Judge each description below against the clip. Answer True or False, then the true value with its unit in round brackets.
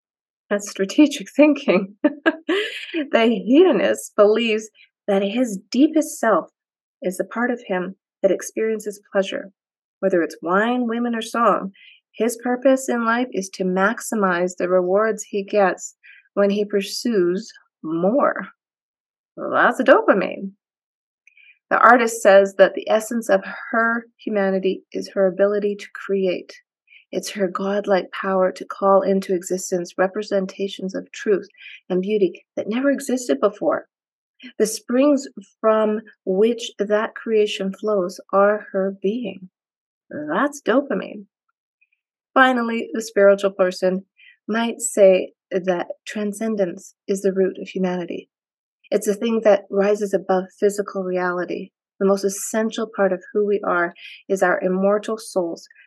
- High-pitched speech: True (205 Hz)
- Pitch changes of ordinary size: True (3.3 semitones)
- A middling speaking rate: False (130 wpm)